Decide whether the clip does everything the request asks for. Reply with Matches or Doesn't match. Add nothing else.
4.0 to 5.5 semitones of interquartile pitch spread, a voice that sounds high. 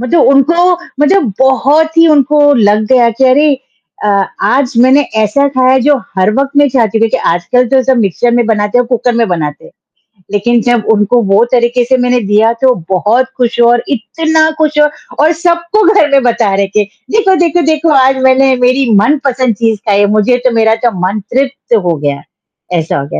Matches